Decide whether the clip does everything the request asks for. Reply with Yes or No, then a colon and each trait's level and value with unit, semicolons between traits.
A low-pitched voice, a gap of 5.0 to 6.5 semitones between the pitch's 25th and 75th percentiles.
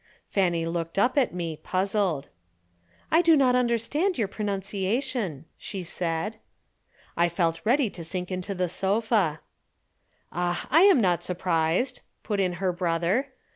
No: high, 190 Hz; average, 5.3 semitones